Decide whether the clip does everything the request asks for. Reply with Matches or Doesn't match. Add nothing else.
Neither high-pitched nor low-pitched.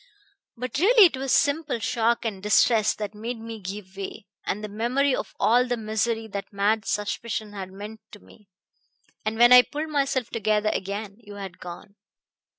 Doesn't match